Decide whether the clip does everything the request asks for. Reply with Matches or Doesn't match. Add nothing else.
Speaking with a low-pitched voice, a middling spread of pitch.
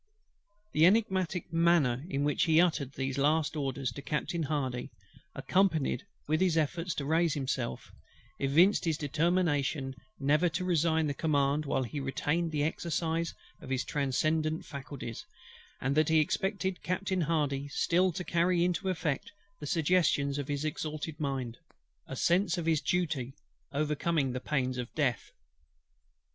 Doesn't match